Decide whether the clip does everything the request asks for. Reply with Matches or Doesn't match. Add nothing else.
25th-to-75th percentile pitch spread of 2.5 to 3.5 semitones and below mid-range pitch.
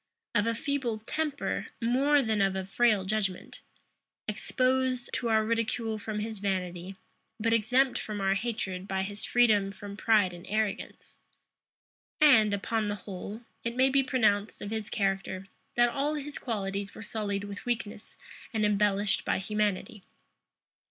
Doesn't match